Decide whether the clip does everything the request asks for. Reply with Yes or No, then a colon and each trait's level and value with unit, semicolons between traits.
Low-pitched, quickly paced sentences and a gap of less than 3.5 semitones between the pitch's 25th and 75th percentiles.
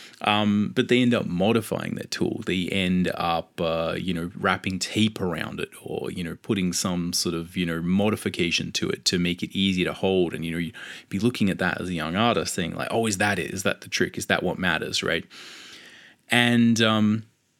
No: very low, 95 Hz; fast, 220 wpm; average, 3.9 semitones